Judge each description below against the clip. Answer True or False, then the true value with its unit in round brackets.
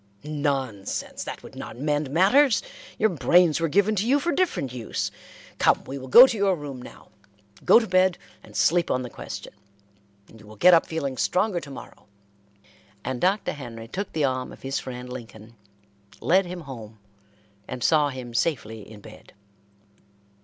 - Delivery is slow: False (175 wpm)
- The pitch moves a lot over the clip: True (6.5 semitones)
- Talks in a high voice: False (145 Hz)